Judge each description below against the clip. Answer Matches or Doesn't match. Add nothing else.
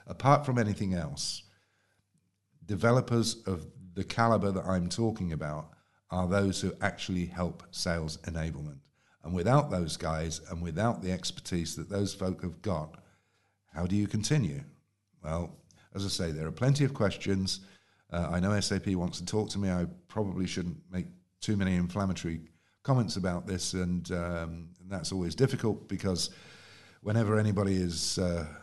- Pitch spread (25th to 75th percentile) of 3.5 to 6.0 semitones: Doesn't match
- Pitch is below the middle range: Matches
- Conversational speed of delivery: Matches